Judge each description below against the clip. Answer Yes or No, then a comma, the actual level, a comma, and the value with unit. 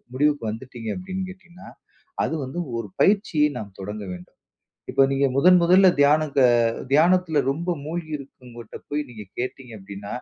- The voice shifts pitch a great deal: Yes, wide, 6.5 semitones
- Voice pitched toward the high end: No, medium, 140 Hz